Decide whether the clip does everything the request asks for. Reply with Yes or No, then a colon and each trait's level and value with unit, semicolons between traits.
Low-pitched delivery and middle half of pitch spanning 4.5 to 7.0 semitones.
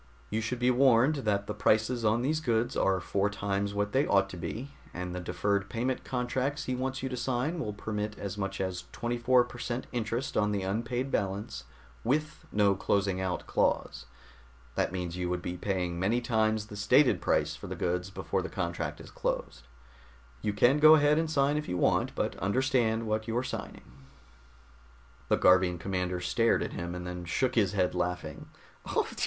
Yes: low, 105 Hz; average, 4.9 semitones